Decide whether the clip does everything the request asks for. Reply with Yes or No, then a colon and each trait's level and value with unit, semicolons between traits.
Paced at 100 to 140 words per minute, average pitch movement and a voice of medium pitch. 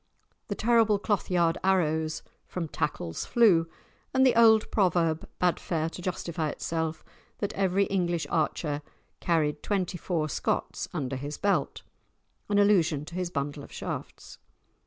Yes: slow, 135 wpm; average, 4.0 semitones; medium, 175 Hz